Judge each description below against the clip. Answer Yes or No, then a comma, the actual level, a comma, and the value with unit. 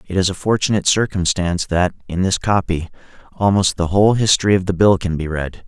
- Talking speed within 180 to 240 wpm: Yes, average, 200 wpm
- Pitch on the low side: Yes, very low, 95 Hz